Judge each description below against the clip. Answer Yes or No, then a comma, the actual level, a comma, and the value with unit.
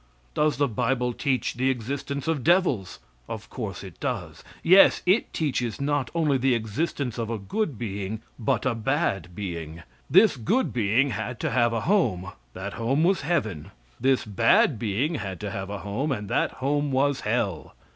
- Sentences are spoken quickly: No, average, 175 wpm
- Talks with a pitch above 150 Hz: No, low, 125 Hz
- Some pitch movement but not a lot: No, wide, 5.7 semitones